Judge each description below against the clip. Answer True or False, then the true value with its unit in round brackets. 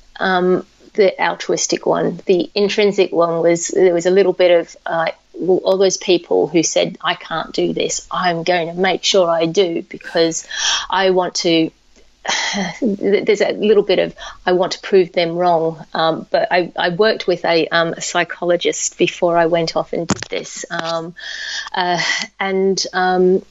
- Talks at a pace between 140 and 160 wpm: False (170 wpm)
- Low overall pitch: False (180 Hz)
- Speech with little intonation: True (2.3 semitones)